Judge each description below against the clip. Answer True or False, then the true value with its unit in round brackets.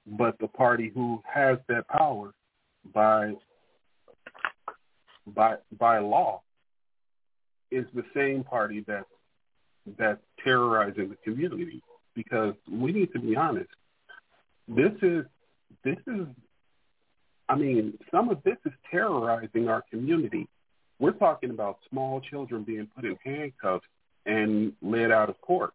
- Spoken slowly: True (125 wpm)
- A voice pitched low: True (120 Hz)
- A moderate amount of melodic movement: False (6.1 semitones)